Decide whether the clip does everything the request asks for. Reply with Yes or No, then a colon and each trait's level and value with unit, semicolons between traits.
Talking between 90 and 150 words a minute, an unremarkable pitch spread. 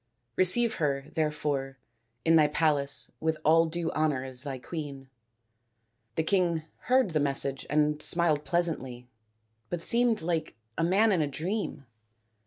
Yes: average, 145 wpm; average, 3.4 semitones